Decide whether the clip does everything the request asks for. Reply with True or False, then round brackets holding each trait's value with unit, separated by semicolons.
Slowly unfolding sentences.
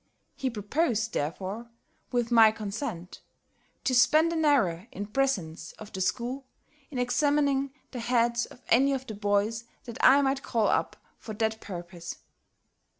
False (150 wpm)